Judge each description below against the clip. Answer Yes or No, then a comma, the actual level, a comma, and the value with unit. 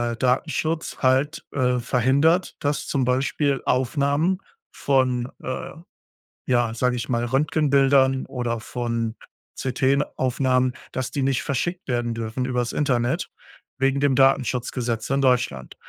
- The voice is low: Yes, low, 130 Hz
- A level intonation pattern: Yes, narrow, 2.3 semitones